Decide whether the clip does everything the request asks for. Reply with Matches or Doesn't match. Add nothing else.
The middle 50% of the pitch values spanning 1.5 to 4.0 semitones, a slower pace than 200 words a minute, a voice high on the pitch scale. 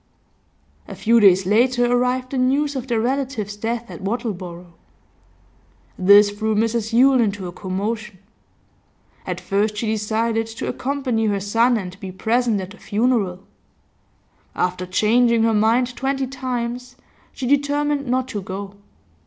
Matches